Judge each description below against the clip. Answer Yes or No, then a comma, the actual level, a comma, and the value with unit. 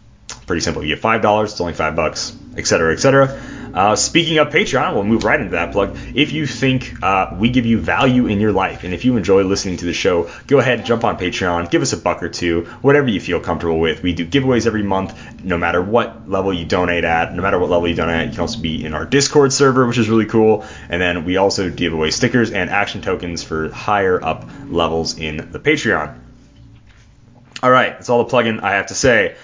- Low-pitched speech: Yes, low, 105 Hz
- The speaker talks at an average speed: No, fast, 245 wpm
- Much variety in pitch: Yes, wide, 6.2 semitones